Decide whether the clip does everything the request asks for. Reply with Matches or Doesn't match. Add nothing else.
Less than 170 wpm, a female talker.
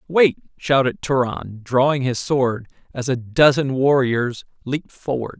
Doesn't match